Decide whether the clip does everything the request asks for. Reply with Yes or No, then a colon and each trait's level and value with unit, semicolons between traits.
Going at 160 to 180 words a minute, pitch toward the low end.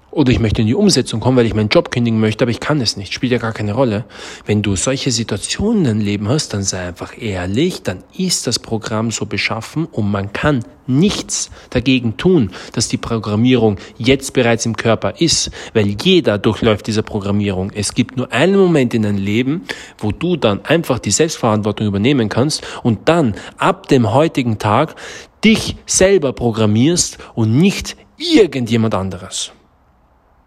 Yes: average, 175 wpm; low, 115 Hz